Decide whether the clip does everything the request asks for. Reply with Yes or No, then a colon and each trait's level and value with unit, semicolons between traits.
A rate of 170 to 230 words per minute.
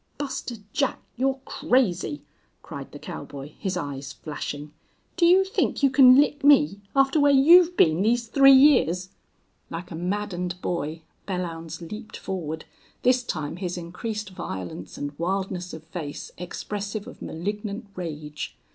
No: average, 140 wpm